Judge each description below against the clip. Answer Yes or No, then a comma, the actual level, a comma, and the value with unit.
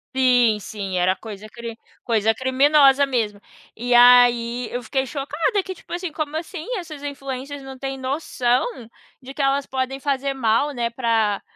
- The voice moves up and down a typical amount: Yes, average, 3.2 semitones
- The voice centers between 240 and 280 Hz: Yes, very high, 260 Hz